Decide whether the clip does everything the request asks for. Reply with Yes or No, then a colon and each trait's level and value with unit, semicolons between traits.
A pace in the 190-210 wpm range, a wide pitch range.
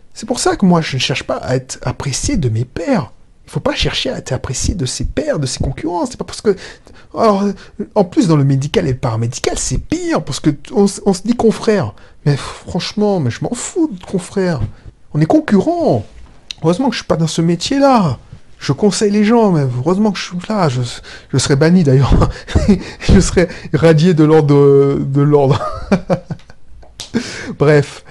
Yes: average, 205 wpm; wide, 7.2 semitones